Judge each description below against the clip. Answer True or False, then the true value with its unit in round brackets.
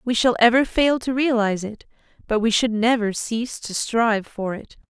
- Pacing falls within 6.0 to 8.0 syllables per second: False (5.1 syllables/s)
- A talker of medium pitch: False (230 Hz)